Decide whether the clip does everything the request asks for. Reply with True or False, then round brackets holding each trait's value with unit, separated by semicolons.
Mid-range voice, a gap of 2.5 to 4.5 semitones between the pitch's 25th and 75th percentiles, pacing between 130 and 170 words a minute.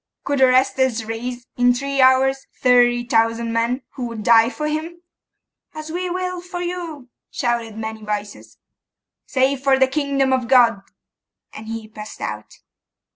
False (255 Hz; 3.5 semitones; 145 wpm)